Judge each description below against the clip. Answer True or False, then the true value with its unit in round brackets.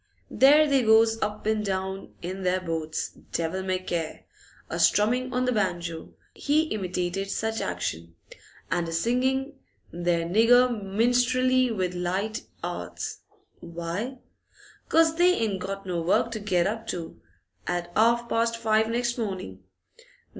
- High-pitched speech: True (210 Hz)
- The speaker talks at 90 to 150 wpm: True (140 wpm)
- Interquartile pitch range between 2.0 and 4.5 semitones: False (5.1 semitones)